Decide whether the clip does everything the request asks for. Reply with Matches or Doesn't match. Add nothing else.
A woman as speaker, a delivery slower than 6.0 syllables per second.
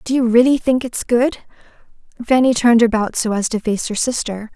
Matches